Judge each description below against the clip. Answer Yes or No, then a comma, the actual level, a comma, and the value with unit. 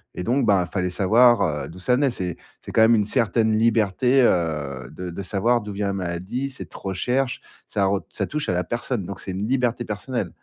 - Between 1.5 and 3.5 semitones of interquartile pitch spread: No, average, 4.7 semitones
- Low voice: Yes, low, 105 Hz